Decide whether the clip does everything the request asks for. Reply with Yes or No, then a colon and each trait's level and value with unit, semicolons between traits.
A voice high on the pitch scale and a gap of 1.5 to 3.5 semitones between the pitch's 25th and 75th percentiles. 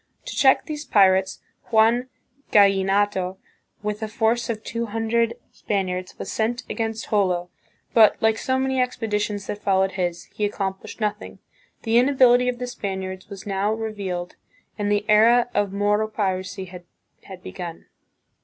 Yes: high, 210 Hz; average, 3.0 semitones